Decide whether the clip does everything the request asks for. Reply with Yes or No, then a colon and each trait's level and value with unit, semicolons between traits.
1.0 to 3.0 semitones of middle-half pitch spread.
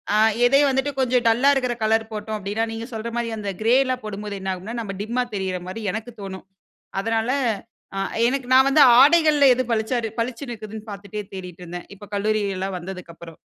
No: average, 3.8 semitones